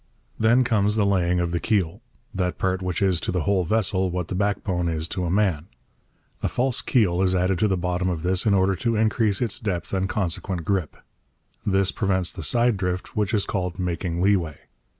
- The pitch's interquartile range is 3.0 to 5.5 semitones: No, narrow, 2.4 semitones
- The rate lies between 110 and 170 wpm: No, fast, 205 wpm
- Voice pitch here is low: Yes, very low, 95 Hz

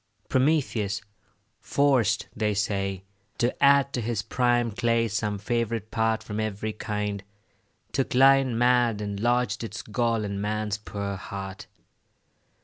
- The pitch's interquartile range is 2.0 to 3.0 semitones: Yes, average, 2.7 semitones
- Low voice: Yes, low, 110 Hz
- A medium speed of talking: No, slow, 130 wpm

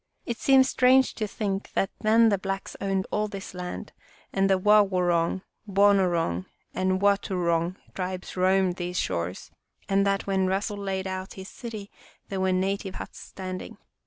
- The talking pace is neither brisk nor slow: Yes, average, 160 wpm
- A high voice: Yes, high, 195 Hz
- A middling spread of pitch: No, narrow, 1.5 semitones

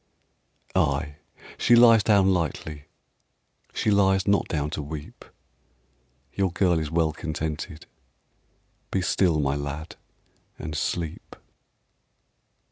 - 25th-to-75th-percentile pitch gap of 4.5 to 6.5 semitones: No, average, 4.1 semitones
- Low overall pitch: Yes, very low, 80 Hz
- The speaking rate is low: Yes, slow, 105 wpm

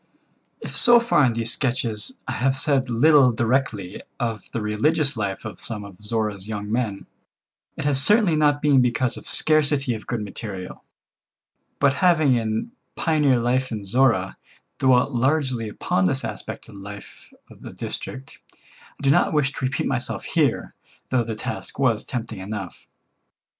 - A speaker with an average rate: Yes, average, 165 wpm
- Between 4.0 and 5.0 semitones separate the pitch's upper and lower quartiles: Yes, average, 4.5 semitones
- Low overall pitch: Yes, low, 125 Hz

